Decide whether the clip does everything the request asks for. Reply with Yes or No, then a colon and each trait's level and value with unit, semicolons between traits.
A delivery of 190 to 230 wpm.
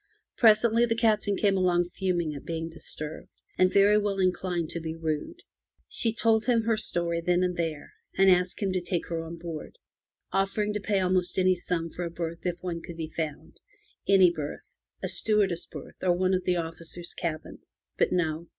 Yes: average, 195 wpm